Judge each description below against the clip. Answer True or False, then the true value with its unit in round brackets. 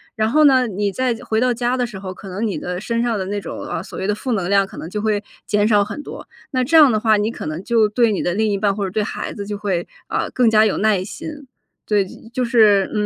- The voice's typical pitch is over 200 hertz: True (210 Hz)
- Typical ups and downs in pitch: True (3.0 semitones)